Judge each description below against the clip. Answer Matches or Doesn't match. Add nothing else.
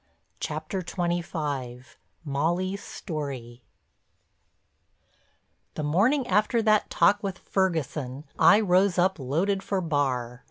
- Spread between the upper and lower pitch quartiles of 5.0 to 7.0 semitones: Matches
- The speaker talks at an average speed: Doesn't match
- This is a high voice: Doesn't match